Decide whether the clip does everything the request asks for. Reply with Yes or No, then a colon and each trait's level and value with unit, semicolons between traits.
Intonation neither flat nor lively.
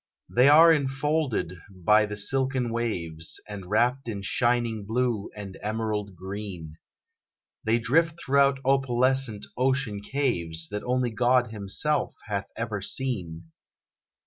Yes: average, 4.5 semitones